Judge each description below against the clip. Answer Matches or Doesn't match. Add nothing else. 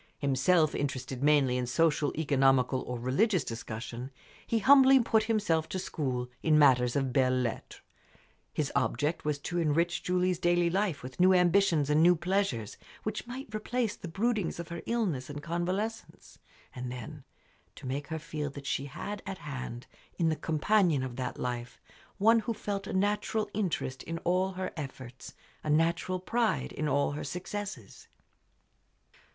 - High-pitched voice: Doesn't match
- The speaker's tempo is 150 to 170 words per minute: Matches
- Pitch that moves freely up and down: Matches